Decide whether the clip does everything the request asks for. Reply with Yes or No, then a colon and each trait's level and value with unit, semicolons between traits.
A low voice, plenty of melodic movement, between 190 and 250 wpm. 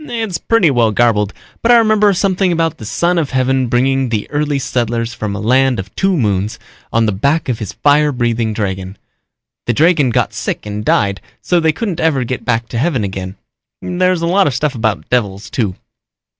Yes: low, 130 Hz; wide, 7.2 semitones; average, 200 wpm